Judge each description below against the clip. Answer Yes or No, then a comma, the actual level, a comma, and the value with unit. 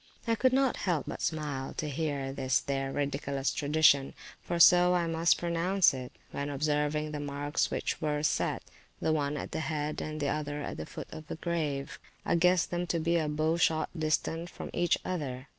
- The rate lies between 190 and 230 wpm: Yes, average, 195 wpm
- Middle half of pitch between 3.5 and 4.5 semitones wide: No, average, 2.9 semitones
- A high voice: No, medium, 155 Hz